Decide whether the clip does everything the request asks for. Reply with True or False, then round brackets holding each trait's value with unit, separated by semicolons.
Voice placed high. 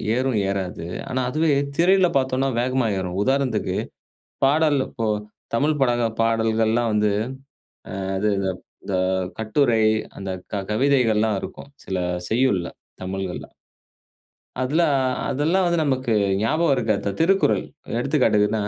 False (125 Hz)